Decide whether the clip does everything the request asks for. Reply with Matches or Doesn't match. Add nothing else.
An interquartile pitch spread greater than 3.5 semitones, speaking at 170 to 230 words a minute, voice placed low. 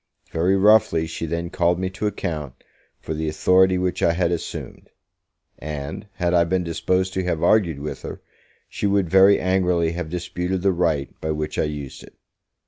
Doesn't match